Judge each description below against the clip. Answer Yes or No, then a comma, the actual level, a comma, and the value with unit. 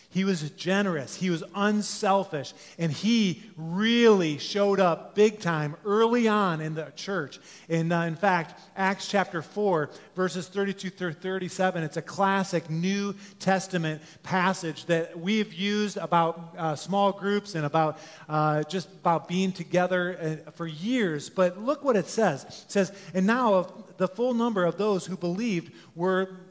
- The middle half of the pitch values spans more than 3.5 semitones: No, average, 3.1 semitones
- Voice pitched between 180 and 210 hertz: Yes, medium, 185 Hz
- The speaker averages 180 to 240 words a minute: No, average, 155 wpm